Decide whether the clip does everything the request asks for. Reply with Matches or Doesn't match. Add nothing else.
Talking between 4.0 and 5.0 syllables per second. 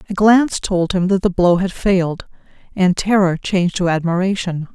Doesn't match